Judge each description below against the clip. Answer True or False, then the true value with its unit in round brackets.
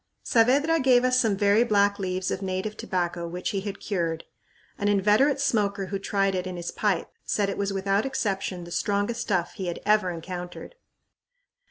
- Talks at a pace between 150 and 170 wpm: False (180 wpm)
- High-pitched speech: True (200 Hz)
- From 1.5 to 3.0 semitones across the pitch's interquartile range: True (2.5 semitones)